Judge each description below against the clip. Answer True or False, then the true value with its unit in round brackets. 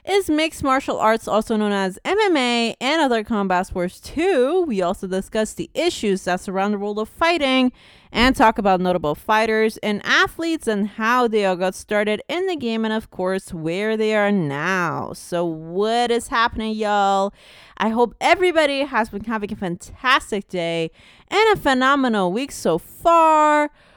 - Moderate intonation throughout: False (5.8 semitones)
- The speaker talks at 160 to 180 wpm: True (170 wpm)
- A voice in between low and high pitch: False (220 Hz)